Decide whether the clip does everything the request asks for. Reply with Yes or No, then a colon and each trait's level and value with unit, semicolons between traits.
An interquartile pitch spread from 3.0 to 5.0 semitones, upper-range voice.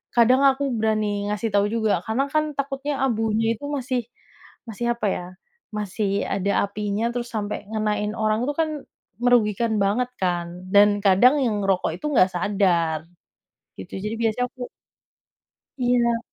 Yes: average, 3.5 semitones; high, 220 Hz